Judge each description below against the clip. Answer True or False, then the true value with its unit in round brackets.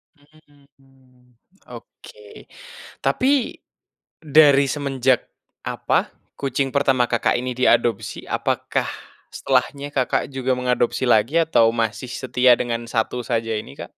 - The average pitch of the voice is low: True (130 Hz)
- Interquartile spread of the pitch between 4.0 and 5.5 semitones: False (2.7 semitones)